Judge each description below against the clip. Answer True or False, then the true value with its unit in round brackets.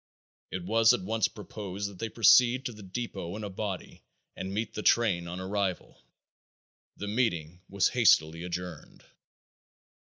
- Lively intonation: False (3.6 semitones)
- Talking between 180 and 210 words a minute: False (150 wpm)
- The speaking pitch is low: True (100 Hz)